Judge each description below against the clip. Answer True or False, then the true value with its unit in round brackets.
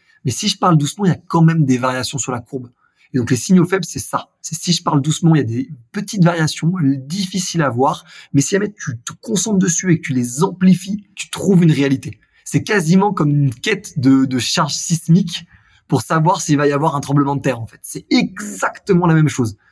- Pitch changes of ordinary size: True (4.9 semitones)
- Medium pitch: True (160 Hz)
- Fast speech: True (240 wpm)